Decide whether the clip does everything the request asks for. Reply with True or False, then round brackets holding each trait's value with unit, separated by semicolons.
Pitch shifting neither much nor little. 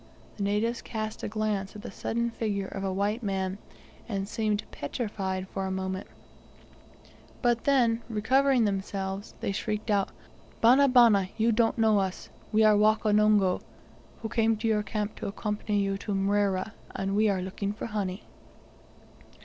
False (2.3 semitones)